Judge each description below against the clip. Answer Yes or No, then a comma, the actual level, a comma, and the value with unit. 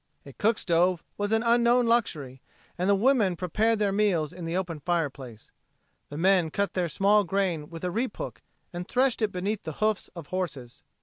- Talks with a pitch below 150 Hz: No, medium, 185 Hz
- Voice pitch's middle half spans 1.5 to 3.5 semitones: No, average, 4.3 semitones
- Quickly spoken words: No, average, 190 wpm